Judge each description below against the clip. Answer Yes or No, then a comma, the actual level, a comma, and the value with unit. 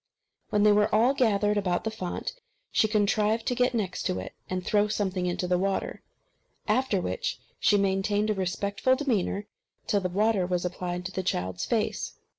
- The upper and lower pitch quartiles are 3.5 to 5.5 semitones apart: No, average, 2.8 semitones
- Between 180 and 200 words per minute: Yes, average, 185 wpm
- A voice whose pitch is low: No, high, 200 Hz